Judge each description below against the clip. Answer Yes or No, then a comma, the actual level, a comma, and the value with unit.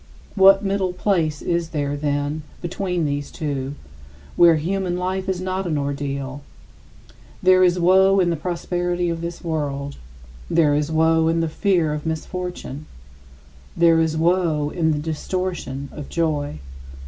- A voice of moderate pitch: Yes, medium, 165 Hz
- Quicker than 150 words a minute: No, average, 145 wpm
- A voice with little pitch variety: No, average, 3.4 semitones